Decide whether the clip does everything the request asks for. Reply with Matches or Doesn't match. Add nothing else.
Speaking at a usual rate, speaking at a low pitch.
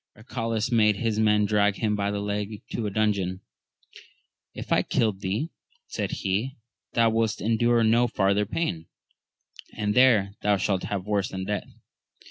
Matches